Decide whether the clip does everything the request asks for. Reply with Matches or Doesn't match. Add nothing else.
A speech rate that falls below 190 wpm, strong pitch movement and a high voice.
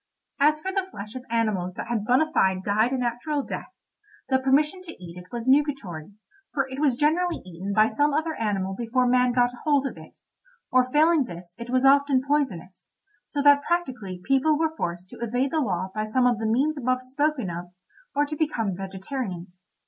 Doesn't match